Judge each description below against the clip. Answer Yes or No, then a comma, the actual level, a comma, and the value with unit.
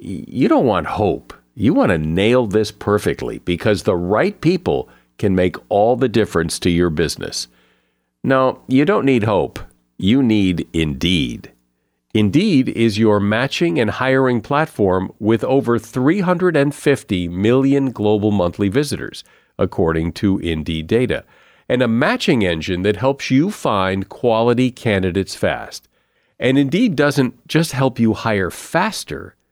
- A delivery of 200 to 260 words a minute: No, slow, 135 wpm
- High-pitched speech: No, low, 110 Hz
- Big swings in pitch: Yes, wide, 7.0 semitones